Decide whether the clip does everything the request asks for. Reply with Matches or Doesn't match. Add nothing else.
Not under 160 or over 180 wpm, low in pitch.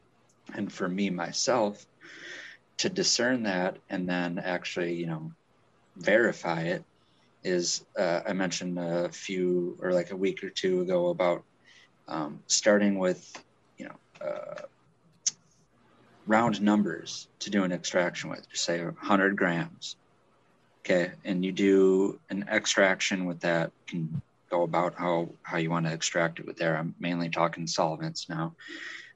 Doesn't match